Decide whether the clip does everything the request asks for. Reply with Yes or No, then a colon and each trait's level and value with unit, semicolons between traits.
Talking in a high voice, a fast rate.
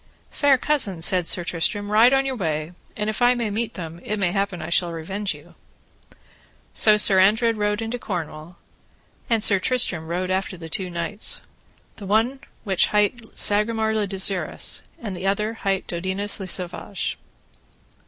No: high, 200 Hz; average, 165 wpm